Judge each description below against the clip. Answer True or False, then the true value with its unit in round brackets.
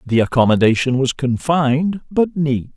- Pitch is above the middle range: False (140 Hz)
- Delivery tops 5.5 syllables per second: False (4.7 syllables/s)